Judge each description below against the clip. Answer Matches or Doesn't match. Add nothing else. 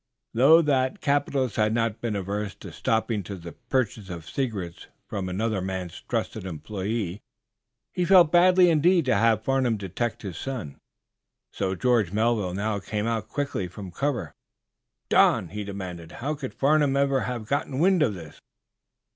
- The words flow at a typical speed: Matches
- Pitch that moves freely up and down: Matches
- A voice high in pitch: Doesn't match